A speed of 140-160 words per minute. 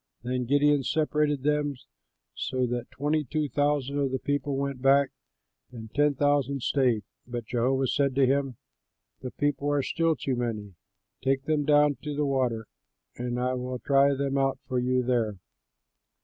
No: average, 170 wpm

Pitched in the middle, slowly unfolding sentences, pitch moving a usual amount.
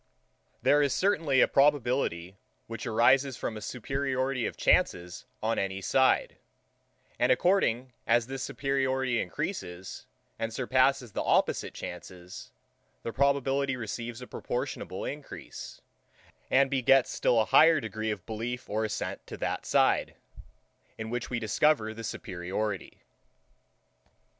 No: low, 120 Hz; slow, 125 wpm; average, 3.7 semitones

